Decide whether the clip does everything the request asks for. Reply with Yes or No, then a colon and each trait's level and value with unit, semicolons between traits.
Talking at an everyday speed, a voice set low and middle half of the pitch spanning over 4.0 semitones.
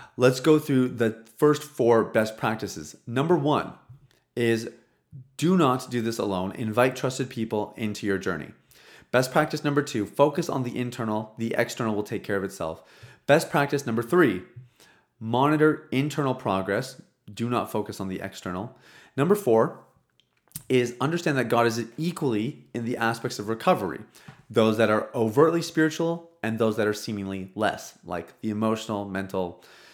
Yes: average, 155 wpm; low, 120 Hz; average, 4.7 semitones